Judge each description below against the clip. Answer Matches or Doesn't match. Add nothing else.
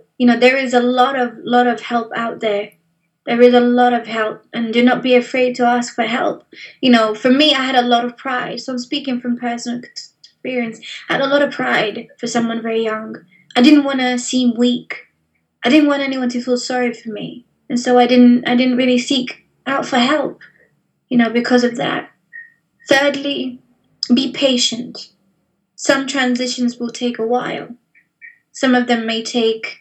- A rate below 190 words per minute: Doesn't match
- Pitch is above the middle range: Matches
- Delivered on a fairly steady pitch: Matches